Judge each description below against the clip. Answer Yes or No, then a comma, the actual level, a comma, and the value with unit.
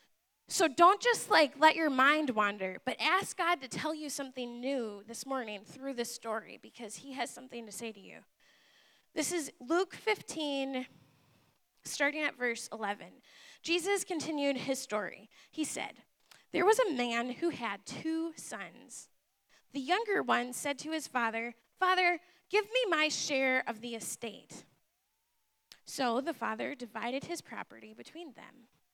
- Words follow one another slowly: No, average, 155 wpm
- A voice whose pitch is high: Yes, very high, 270 Hz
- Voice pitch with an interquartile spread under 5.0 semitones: No, wide, 5.6 semitones